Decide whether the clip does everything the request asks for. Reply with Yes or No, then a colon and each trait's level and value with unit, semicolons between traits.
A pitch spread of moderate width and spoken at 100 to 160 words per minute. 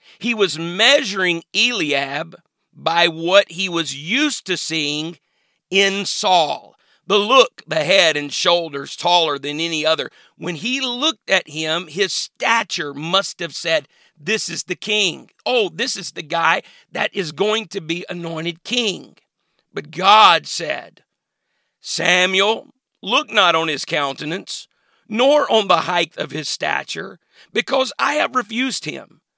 Yes: average, 5.0 semitones; average, 145 wpm